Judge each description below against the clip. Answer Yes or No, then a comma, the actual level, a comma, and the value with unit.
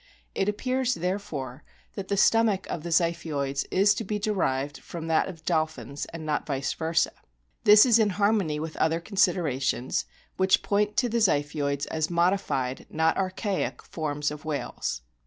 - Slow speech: No, average, 155 wpm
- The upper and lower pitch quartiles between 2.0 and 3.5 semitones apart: No, average, 5.2 semitones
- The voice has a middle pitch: Yes, medium, 170 Hz